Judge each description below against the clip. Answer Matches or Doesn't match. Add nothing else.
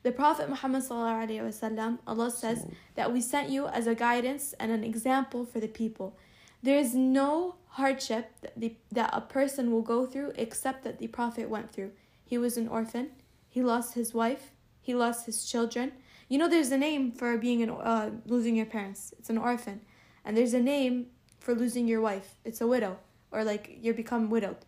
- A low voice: Doesn't match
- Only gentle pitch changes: Matches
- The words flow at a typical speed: Matches